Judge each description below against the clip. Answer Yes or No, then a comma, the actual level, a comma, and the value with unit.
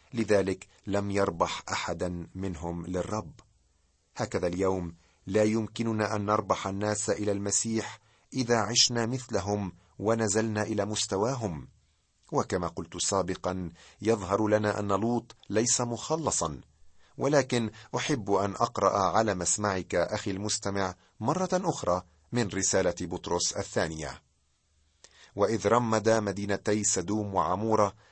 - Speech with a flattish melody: No, average, 3.4 semitones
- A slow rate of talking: No, average, 105 wpm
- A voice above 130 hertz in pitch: No, low, 100 Hz